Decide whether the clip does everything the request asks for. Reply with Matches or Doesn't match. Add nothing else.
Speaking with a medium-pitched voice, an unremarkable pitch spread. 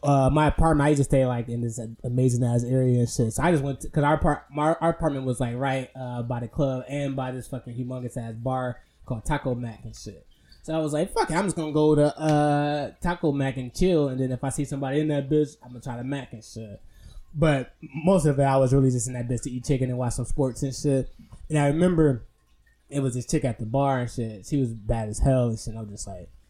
Doesn't match